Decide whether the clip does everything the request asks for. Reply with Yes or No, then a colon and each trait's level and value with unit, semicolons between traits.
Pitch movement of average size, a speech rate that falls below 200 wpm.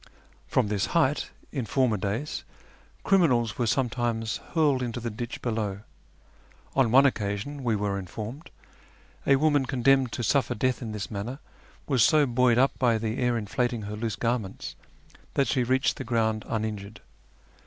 Yes: average, 3.4 semitones; average, 160 wpm